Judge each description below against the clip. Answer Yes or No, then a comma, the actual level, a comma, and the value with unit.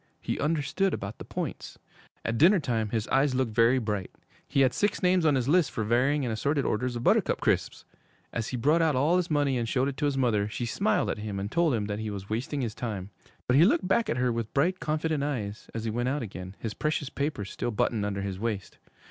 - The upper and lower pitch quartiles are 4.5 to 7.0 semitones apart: Yes, average, 5.3 semitones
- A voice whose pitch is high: No, low, 125 Hz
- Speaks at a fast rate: Yes, fast, 240 wpm